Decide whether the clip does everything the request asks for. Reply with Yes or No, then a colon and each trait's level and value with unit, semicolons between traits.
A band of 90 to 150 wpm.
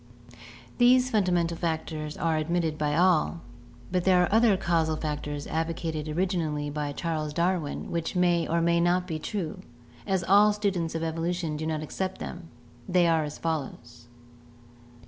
No: average, 165 wpm